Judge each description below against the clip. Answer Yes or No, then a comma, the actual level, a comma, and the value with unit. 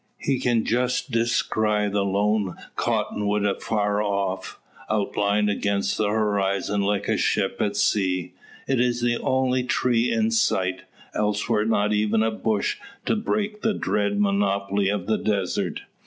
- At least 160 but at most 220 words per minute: No, average, 140 wpm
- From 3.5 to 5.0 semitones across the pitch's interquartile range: No, narrow, 2.6 semitones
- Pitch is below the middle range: Yes, low, 105 Hz